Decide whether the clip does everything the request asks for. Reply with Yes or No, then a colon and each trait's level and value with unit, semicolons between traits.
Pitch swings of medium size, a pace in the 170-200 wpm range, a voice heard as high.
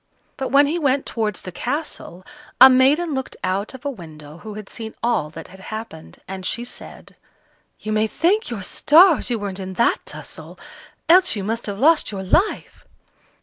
No: wide, 6.6 semitones; average, 185 wpm; high, 225 Hz